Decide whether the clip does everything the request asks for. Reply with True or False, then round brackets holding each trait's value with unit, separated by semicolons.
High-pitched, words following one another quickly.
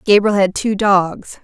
False (200 Hz; 170 wpm)